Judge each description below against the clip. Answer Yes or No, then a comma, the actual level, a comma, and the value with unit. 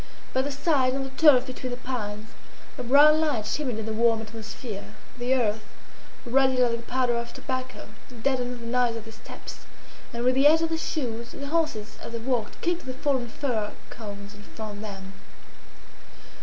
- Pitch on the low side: No, high, 245 Hz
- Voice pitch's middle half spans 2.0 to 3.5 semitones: Yes, average, 3.1 semitones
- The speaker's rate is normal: Yes, average, 190 wpm